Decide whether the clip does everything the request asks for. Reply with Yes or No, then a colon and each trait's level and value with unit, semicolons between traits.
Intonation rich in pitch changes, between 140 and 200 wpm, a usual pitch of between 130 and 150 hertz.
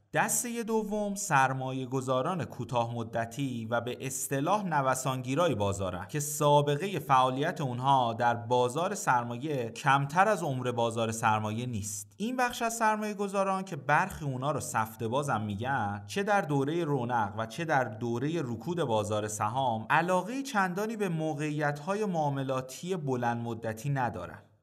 No: wide, 6.5 semitones; average, 130 wpm; low, 135 Hz